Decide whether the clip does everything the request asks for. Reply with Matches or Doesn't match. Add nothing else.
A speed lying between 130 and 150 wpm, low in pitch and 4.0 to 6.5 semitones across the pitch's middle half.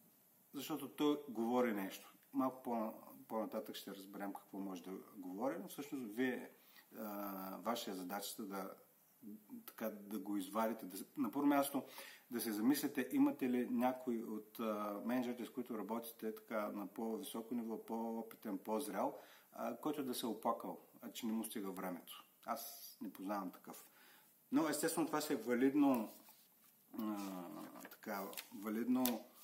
Matches